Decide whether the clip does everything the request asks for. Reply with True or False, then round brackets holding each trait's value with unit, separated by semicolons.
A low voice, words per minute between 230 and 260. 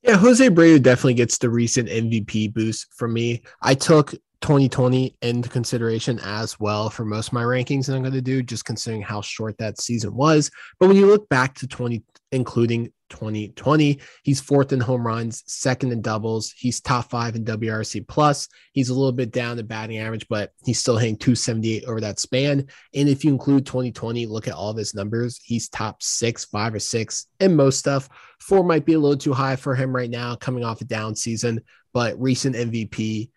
False (120 Hz; 205 wpm)